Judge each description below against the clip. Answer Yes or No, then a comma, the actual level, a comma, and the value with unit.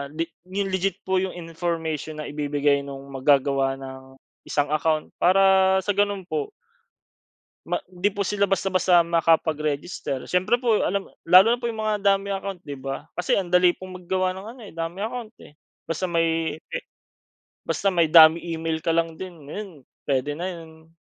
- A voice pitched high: No, medium, 170 Hz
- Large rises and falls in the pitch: No, average, 3.8 semitones